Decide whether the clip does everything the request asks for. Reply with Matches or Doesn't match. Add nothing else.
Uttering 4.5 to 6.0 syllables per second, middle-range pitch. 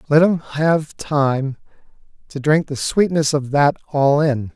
Doesn't match